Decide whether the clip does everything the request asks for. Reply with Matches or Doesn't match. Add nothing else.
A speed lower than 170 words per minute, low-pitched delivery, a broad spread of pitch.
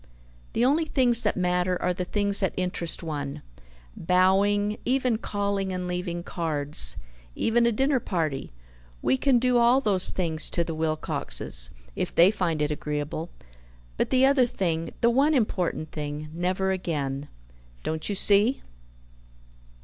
Doesn't match